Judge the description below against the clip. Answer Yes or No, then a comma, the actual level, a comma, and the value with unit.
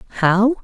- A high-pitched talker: Yes, high, 215 Hz